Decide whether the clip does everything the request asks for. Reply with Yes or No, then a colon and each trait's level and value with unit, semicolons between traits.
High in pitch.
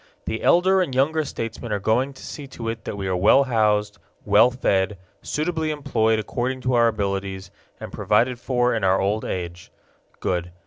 No: low, 115 Hz